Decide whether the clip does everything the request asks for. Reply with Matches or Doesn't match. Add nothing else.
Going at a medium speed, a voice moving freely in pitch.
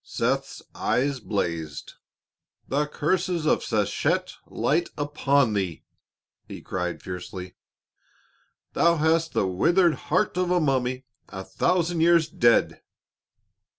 Doesn't match